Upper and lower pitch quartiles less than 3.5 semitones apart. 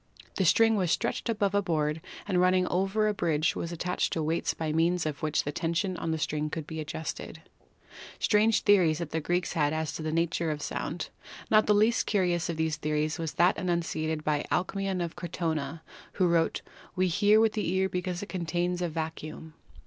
Yes: average, 2.9 semitones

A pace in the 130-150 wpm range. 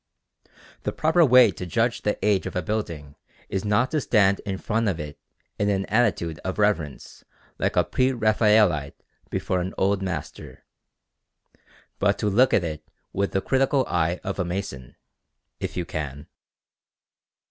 No: average, 160 wpm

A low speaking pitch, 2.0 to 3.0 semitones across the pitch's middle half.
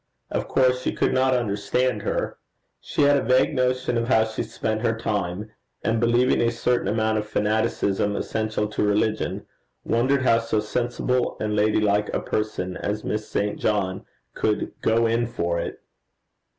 Yes: low, 110 Hz; narrow, 2.5 semitones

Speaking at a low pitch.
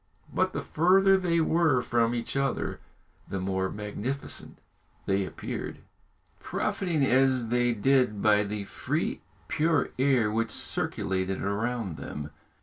Yes: low, 120 Hz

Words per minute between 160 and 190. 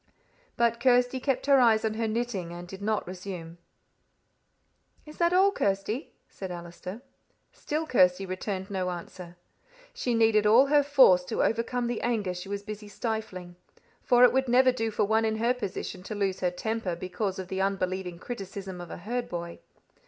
Yes: average, 175 wpm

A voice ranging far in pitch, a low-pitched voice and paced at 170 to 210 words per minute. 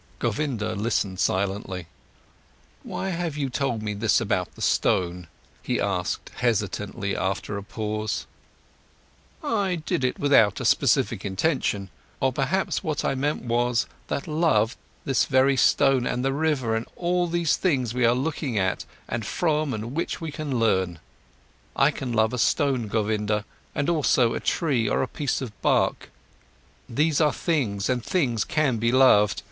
No: wide, 5.7 semitones; low, 125 Hz; average, 155 wpm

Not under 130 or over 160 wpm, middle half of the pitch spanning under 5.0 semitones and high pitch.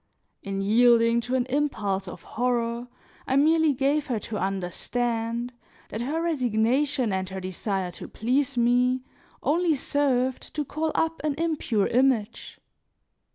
Yes: slow, 135 wpm; average, 4.3 semitones; high, 245 Hz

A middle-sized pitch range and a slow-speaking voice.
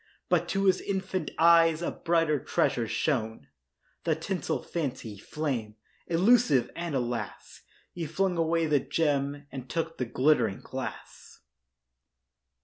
Yes: average, 4.7 semitones; slow, 125 wpm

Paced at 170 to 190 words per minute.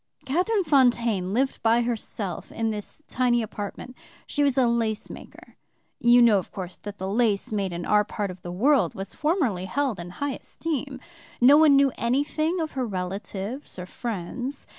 Yes: average, 175 wpm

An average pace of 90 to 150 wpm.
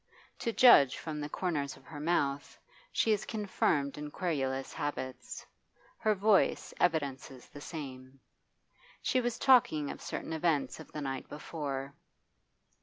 Yes: slow, 135 wpm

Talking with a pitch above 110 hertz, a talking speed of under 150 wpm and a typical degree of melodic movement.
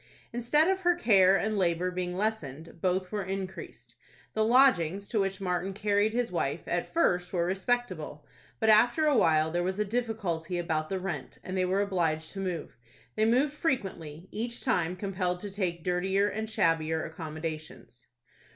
No: high, 190 Hz; average, 170 wpm; average, 4.2 semitones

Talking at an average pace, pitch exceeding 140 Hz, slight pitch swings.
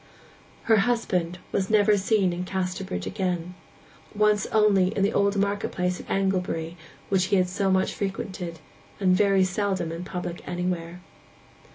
Yes: average, 150 wpm; high, 190 Hz; narrow, 1.9 semitones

